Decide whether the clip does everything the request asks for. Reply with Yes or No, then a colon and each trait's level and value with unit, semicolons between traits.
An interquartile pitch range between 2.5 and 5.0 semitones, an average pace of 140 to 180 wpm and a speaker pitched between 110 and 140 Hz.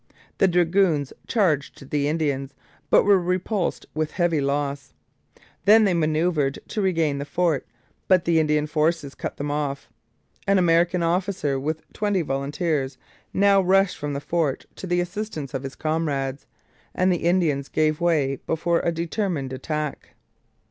No: average, 3.9 semitones; average, 150 wpm; medium, 160 Hz